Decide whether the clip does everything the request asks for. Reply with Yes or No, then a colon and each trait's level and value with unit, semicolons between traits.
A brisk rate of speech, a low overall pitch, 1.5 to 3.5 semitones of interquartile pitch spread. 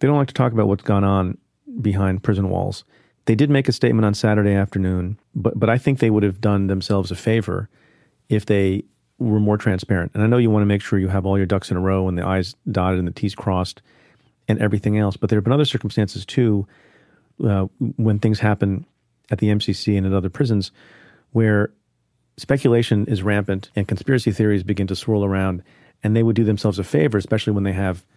Yes: fast, 220 wpm; low, 105 Hz; average, 2.7 semitones